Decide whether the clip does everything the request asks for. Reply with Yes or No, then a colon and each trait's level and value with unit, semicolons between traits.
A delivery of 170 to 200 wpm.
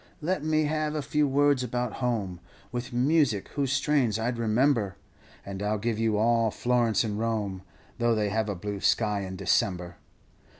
Yes: average, 180 wpm